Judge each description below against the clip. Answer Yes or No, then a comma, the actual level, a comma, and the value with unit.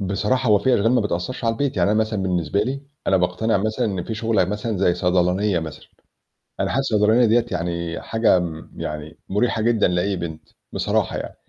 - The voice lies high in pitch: No, low, 100 Hz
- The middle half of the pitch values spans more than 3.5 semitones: Yes, average, 4.2 semitones